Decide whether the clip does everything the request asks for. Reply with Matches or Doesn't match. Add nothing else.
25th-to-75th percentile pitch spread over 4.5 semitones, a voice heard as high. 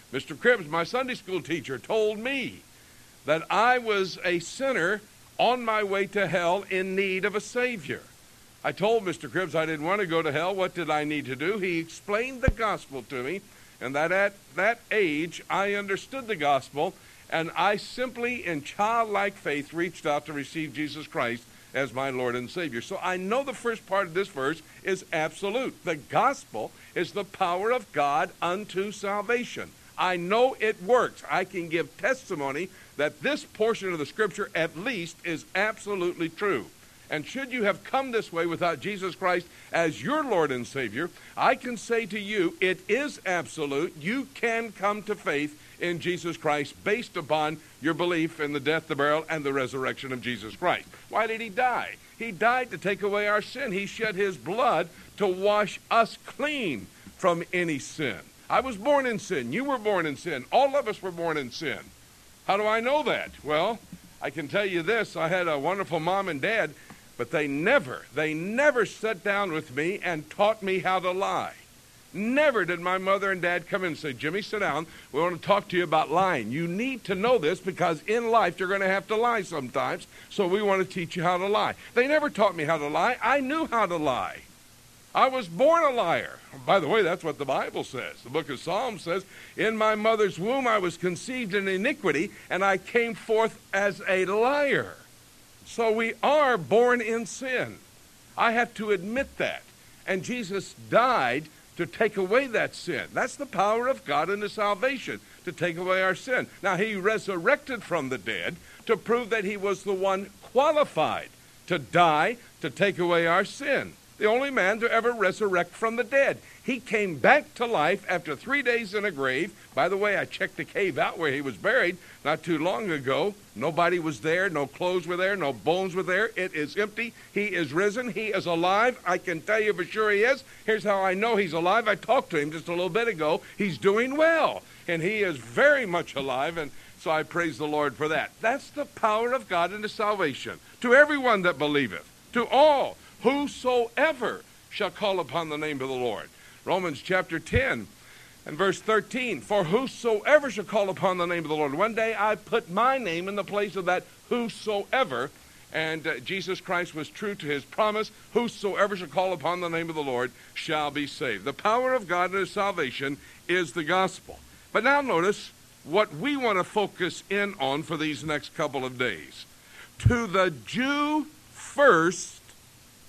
Matches